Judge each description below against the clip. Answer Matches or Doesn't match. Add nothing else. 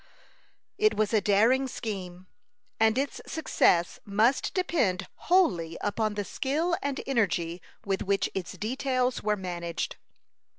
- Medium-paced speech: Doesn't match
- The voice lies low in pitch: Doesn't match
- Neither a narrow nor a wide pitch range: Doesn't match